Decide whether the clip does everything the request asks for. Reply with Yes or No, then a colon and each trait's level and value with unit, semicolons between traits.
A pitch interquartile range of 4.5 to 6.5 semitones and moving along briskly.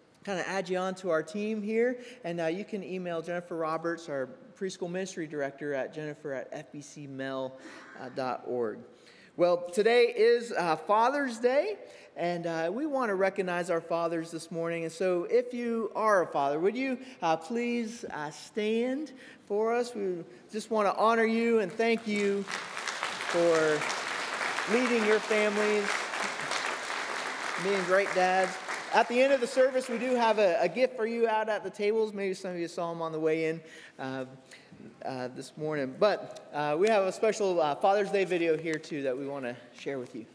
No: average, 5.3 semitones; average, 185 wpm